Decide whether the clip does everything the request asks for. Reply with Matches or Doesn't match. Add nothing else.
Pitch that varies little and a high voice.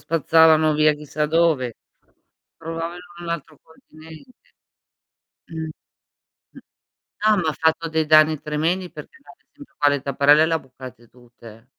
Doesn't match